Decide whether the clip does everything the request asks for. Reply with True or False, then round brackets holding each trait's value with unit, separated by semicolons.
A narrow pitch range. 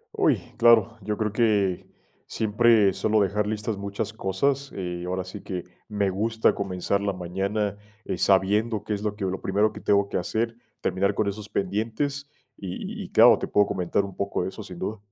True (2.2 semitones)